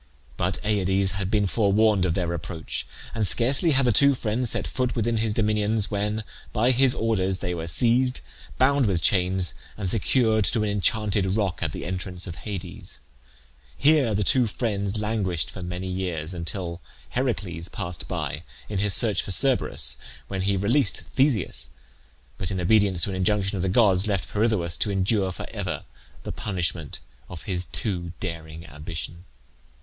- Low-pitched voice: Yes, low, 100 Hz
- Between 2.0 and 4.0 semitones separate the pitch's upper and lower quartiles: Yes, average, 3.7 semitones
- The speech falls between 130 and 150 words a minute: No, average, 165 wpm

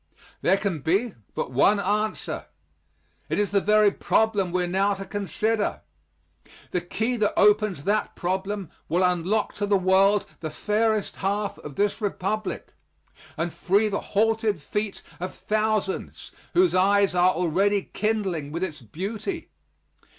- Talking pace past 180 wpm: No, average, 145 wpm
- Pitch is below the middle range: No, high, 200 Hz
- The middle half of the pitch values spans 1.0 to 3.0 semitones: Yes, average, 2.7 semitones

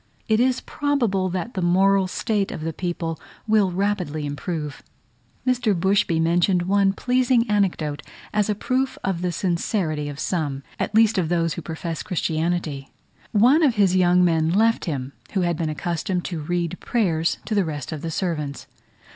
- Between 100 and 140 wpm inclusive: No, average, 170 wpm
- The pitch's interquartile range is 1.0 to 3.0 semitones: No, average, 4.2 semitones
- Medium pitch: Yes, medium, 180 Hz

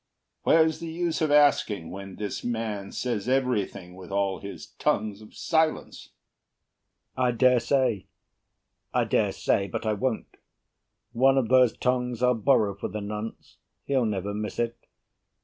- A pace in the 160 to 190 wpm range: No, average, 150 wpm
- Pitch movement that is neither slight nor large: Yes, average, 4.2 semitones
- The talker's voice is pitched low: Yes, low, 115 Hz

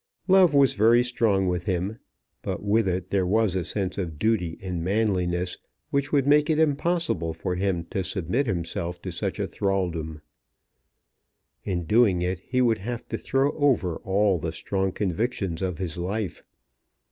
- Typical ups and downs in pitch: Yes, average, 4.7 semitones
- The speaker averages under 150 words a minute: No, average, 160 wpm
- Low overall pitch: Yes, very low, 95 Hz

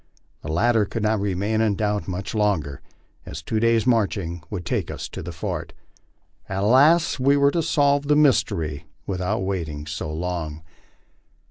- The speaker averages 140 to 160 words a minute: Yes, average, 155 wpm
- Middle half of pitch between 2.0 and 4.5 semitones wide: No, wide, 5.4 semitones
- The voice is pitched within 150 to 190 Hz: No, low, 100 Hz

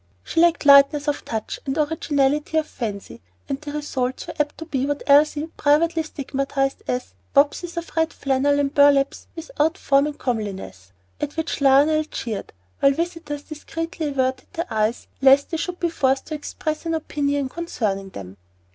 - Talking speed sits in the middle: Yes, average, 165 wpm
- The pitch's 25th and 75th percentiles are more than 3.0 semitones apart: No, average, 2.7 semitones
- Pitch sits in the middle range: No, very high, 285 Hz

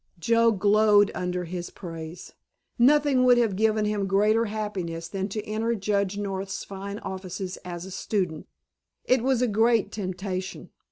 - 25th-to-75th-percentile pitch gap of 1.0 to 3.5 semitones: Yes, average, 2.9 semitones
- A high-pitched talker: Yes, high, 200 Hz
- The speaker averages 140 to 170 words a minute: Yes, average, 150 wpm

